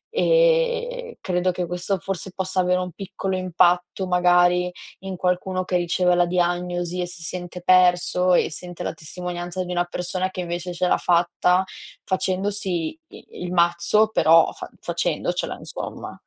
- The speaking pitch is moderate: Yes, medium, 180 Hz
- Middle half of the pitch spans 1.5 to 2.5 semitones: No, narrow, 1.1 semitones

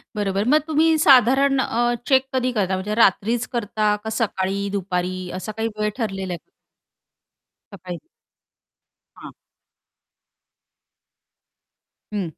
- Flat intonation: No, average, 4.4 semitones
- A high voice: Yes, high, 210 Hz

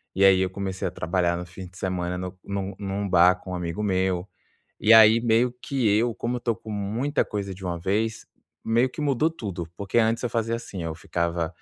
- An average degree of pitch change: Yes, average, 3.8 semitones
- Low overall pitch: Yes, low, 100 Hz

